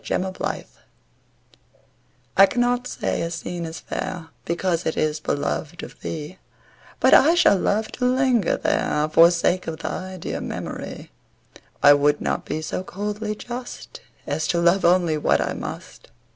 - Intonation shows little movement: No, average, 4.5 semitones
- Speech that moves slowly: No, average, 150 wpm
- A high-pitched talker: No, medium, 175 Hz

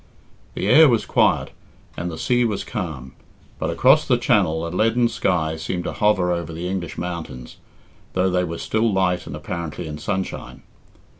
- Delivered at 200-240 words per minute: No, average, 170 wpm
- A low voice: Yes, very low, 90 Hz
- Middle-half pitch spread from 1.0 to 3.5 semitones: No, average, 3.9 semitones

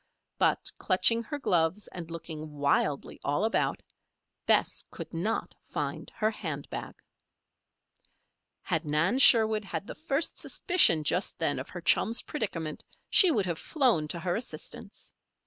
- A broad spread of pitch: Yes, wide, 6.1 semitones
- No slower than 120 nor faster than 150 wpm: Yes, average, 140 wpm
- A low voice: No, medium, 185 Hz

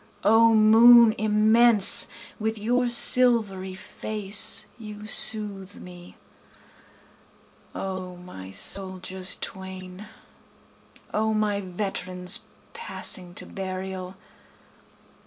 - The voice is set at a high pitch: Yes, high, 200 Hz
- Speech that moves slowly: Yes, slow, 80 wpm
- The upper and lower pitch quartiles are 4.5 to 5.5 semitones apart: No, average, 2.7 semitones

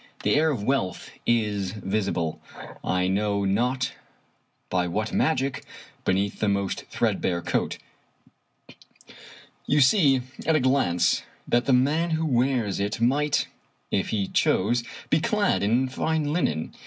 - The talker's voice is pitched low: Yes, low, 120 Hz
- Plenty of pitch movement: Yes, wide, 5.9 semitones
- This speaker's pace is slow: Yes, slow, 130 wpm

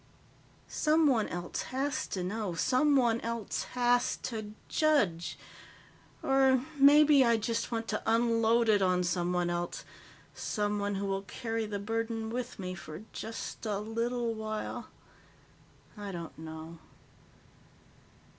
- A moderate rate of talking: No, slow, 120 wpm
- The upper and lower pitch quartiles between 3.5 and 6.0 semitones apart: Yes, average, 3.8 semitones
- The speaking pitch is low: No, high, 225 Hz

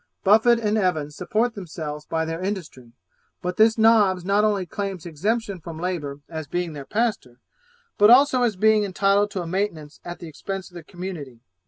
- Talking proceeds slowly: No, average, 180 wpm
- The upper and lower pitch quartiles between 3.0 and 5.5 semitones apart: Yes, average, 4.5 semitones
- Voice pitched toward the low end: No, medium, 185 Hz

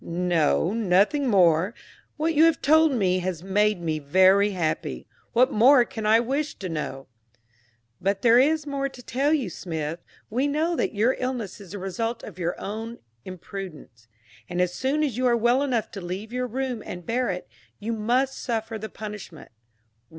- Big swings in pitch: Yes, wide, 5.8 semitones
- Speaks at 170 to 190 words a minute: Yes, average, 180 wpm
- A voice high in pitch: Yes, high, 215 Hz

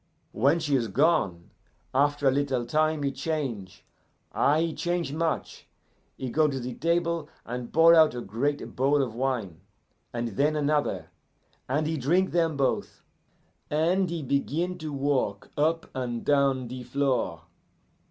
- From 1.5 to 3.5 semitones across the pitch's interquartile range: No, average, 4.1 semitones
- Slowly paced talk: No, average, 150 wpm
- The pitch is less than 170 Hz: Yes, medium, 140 Hz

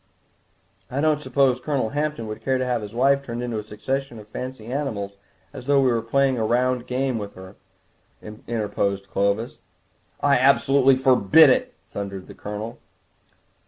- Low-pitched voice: Yes, low, 125 Hz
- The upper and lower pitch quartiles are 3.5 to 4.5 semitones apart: Yes, average, 4.1 semitones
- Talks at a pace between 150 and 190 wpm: Yes, average, 160 wpm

